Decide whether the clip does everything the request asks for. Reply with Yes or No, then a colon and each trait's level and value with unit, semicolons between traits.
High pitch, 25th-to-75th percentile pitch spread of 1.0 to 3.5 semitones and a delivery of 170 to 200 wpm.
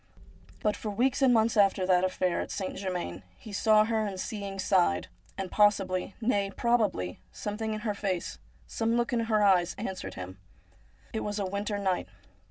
Yes: high, 205 Hz; average, 2.9 semitones; average, 180 wpm